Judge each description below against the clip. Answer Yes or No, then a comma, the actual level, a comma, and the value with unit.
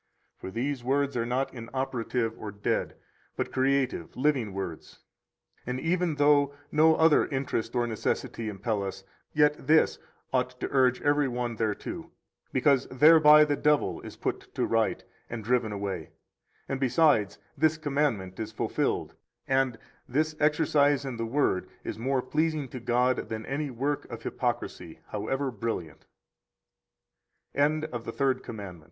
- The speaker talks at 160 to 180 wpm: No, slow, 135 wpm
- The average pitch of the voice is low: Yes, low, 130 Hz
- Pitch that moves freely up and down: No, average, 4.2 semitones